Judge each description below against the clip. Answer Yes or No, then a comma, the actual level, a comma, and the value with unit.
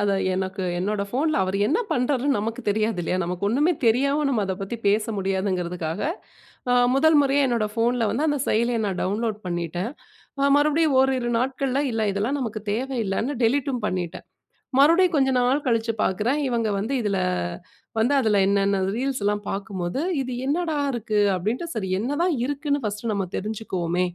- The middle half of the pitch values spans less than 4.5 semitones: No, average, 5.3 semitones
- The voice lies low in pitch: No, high, 225 Hz